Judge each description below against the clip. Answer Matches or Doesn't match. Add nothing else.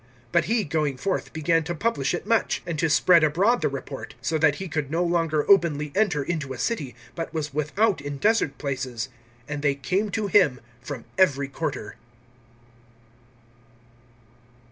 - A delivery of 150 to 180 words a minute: Matches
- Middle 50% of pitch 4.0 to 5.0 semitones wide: Matches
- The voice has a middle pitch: Matches